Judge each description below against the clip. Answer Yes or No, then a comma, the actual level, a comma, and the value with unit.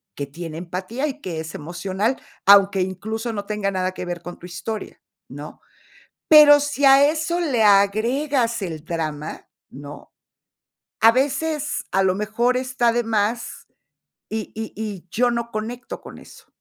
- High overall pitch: Yes, high, 215 Hz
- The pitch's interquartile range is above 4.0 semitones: Yes, wide, 5.4 semitones